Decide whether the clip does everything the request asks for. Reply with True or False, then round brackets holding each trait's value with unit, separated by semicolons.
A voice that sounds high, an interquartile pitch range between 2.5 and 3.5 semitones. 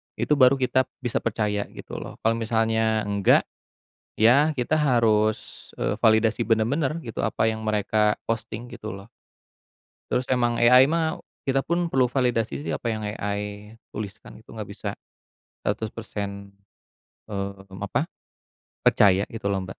False (110 Hz; 2.8 semitones)